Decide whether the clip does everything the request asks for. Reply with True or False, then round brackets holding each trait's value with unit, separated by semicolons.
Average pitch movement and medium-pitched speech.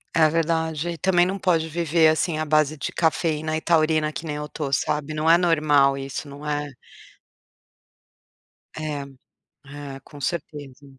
False (1.9 semitones; 155 Hz)